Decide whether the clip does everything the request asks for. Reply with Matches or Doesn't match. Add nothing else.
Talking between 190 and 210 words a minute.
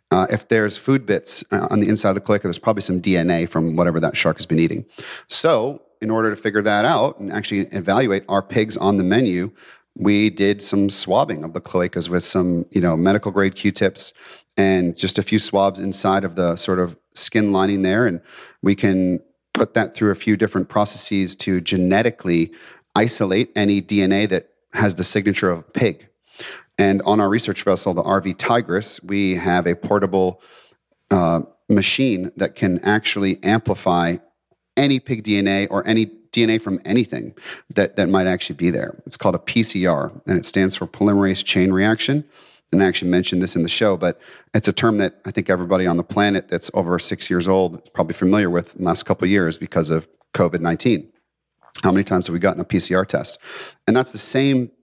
Matches